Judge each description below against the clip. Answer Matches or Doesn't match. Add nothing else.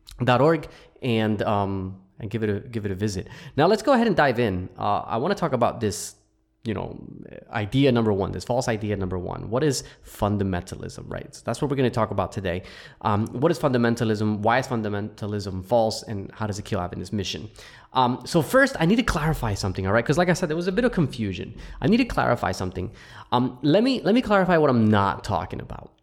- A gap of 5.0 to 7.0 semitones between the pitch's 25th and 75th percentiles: Matches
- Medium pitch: Doesn't match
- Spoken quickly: Matches